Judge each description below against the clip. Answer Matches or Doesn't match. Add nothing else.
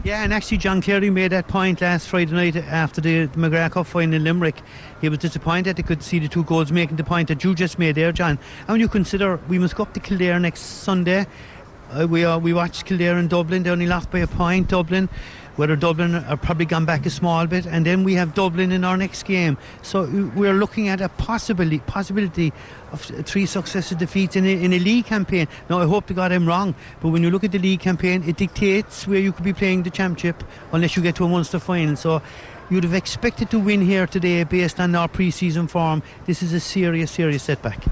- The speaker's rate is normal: Doesn't match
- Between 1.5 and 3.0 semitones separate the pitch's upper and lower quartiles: Matches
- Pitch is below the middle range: Doesn't match